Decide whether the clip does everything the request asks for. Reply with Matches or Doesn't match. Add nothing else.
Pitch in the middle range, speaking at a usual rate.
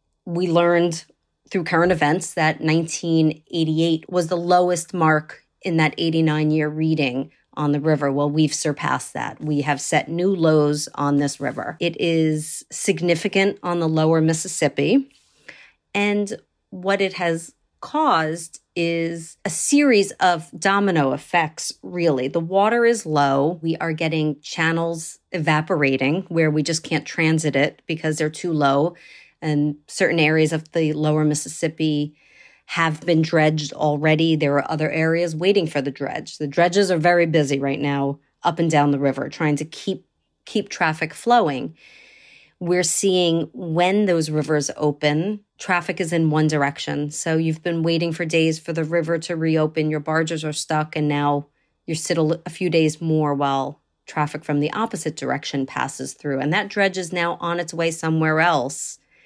Matches